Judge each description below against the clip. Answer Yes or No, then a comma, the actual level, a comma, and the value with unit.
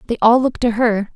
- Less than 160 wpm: No, fast, 260 wpm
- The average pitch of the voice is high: Yes, high, 230 Hz